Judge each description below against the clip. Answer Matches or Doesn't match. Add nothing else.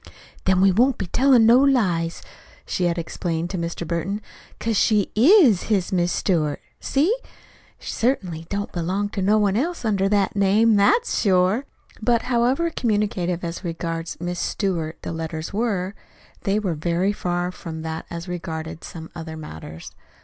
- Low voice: Doesn't match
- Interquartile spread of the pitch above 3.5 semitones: Matches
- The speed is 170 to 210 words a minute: Doesn't match